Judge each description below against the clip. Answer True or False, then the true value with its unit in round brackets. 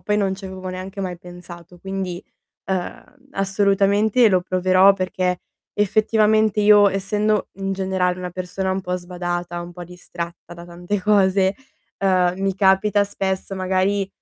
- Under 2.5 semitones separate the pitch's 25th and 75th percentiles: True (1.7 semitones)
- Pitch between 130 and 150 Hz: False (190 Hz)